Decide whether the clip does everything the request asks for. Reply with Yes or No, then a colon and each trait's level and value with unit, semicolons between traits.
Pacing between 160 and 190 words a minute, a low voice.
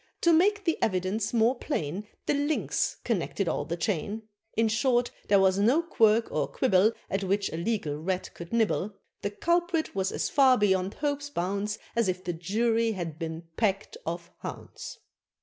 No: average, 170 wpm; high, 205 Hz